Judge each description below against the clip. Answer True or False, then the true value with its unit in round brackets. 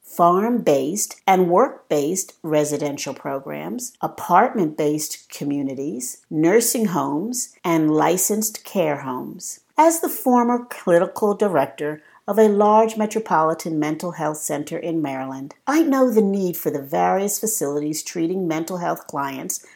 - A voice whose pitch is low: False (170 Hz)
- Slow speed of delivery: True (120 wpm)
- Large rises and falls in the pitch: True (6.3 semitones)